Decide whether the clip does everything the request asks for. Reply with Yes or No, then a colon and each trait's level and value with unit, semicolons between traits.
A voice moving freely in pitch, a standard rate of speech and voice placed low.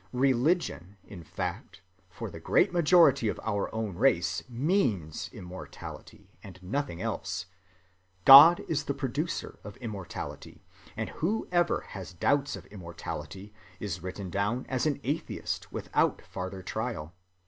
No: wide, 7.4 semitones; slow, 125 wpm; low, 110 Hz